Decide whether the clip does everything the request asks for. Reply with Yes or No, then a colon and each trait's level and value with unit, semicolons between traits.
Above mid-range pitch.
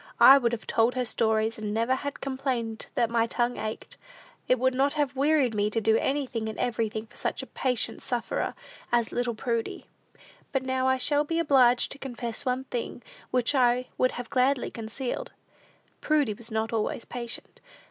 Yes: high, 245 Hz